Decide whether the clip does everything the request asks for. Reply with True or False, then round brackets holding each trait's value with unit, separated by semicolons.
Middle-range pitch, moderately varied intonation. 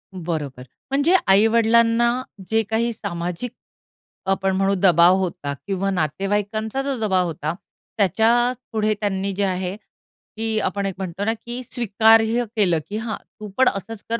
False (205 Hz; 3.2 semitones)